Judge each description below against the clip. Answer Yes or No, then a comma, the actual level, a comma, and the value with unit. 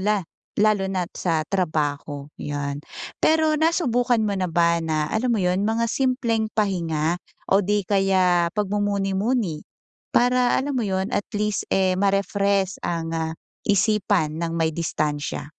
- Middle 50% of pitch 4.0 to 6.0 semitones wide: Yes, average, 4.3 semitones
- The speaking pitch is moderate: No, high, 195 Hz